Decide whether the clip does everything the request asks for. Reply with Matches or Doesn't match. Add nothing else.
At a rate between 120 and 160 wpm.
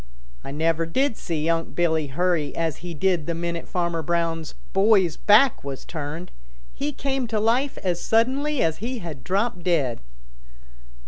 Matches